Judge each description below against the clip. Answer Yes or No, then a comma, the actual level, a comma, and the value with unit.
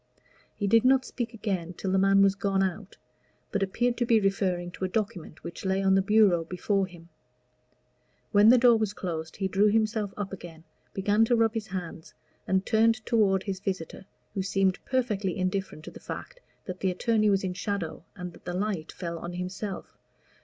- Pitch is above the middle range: Yes, high, 195 Hz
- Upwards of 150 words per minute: Yes, average, 195 wpm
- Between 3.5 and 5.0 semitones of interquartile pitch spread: No, average, 2.7 semitones